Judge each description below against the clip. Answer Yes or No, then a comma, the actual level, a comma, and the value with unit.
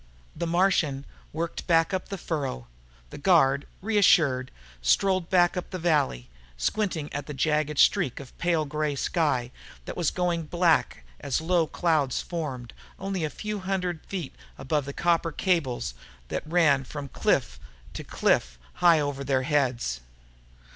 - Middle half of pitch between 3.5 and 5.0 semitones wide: Yes, average, 4.2 semitones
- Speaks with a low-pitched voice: No, medium, 155 Hz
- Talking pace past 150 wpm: No, average, 145 wpm